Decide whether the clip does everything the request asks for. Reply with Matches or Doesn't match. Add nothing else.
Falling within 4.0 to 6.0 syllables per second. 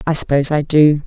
Doesn't match